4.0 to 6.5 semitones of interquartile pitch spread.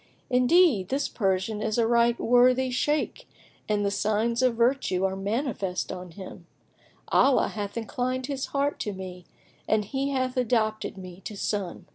Yes: average, 4.4 semitones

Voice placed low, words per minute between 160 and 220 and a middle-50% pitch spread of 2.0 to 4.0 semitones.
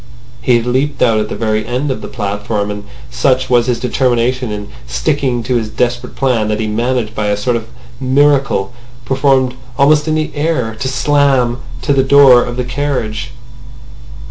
Yes: low, 125 Hz; average, 180 wpm; average, 3.4 semitones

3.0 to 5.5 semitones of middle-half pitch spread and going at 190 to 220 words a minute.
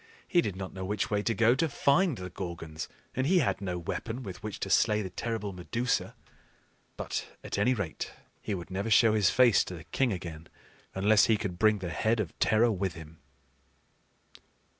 Yes: average, 4.0 semitones; average, 195 wpm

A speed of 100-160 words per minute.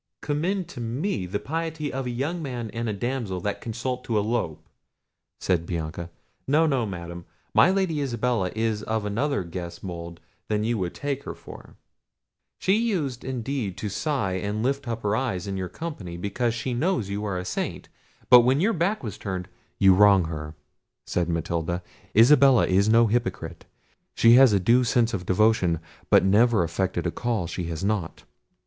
No: average, 175 wpm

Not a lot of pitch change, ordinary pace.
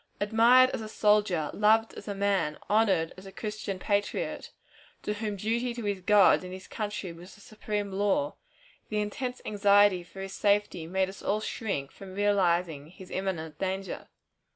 Yes: narrow, 2.2 semitones; average, 170 wpm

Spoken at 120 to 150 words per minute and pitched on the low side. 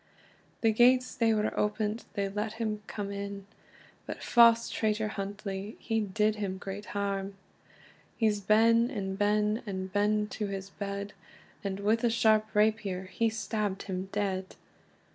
No: average, 145 wpm; high, 210 Hz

